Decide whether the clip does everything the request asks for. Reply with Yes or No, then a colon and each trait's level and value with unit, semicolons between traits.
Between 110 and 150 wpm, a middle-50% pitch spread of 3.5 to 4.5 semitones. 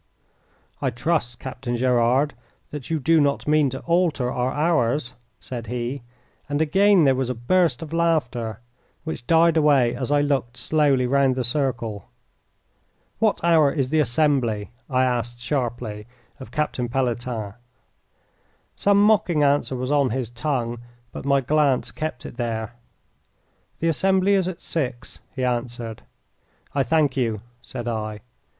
Yes: average, 145 wpm; average, 4.1 semitones